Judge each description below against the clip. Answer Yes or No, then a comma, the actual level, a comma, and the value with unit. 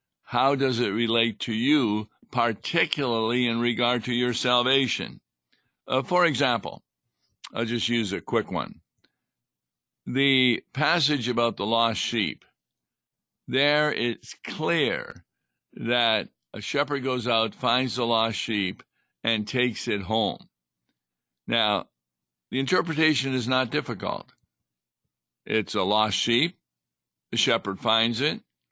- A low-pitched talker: Yes, low, 120 Hz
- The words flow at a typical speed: No, slow, 120 wpm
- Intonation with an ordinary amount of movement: Yes, average, 3.8 semitones